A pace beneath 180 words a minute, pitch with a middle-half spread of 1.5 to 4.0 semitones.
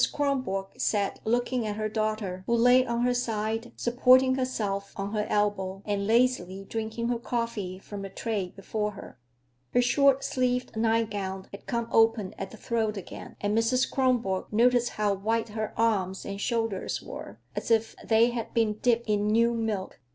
Yes: average, 170 wpm; average, 2.7 semitones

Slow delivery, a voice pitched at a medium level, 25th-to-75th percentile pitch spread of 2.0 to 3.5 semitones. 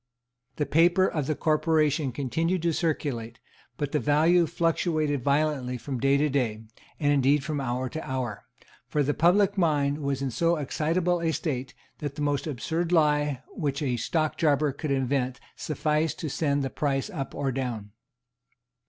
No: average, 160 wpm; medium, 145 Hz; average, 2.9 semitones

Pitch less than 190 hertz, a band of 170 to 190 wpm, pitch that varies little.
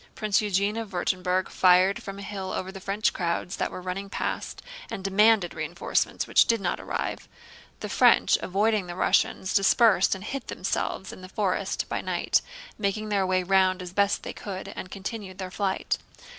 No: high, 195 Hz; average, 180 wpm; narrow, 1.7 semitones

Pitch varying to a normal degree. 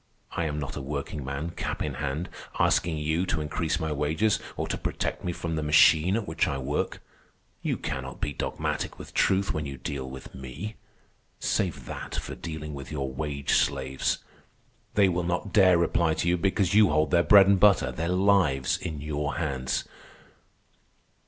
Yes: average, 4.0 semitones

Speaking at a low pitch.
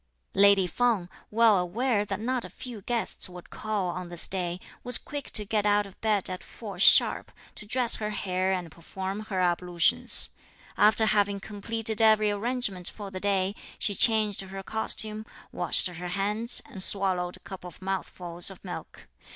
No: high, 200 Hz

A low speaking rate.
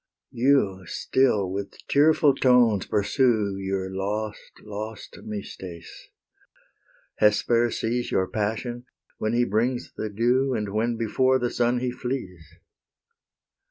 Yes: slow, 115 wpm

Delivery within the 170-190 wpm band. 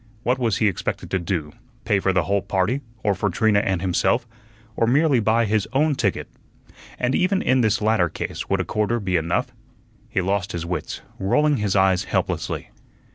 Yes: average, 185 wpm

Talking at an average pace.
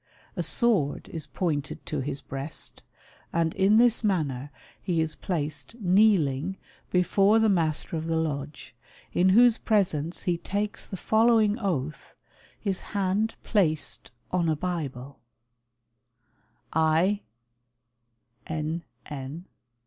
No: slow, 115 wpm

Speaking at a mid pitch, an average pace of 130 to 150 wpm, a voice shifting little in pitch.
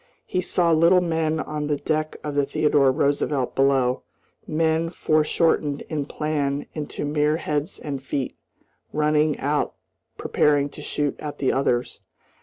Yes: medium, 150 Hz; average, 140 wpm; narrow, 1.6 semitones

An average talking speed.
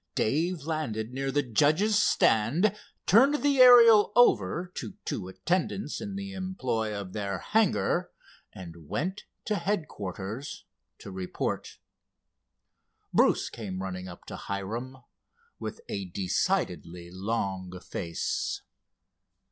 No: slow, 110 wpm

